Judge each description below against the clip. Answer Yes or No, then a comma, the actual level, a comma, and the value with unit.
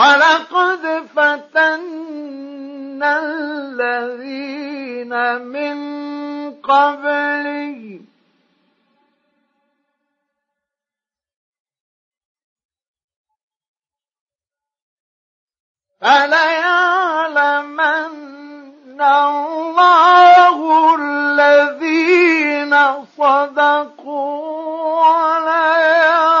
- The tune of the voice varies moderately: No, narrow, 1.9 semitones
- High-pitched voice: Yes, very high, 290 Hz